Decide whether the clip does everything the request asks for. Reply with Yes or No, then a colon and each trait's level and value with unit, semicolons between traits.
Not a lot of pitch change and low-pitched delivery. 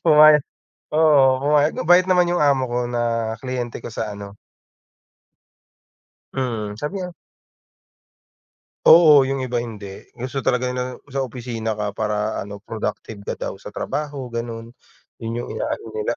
No: average, 4.4 semitones; low, 125 Hz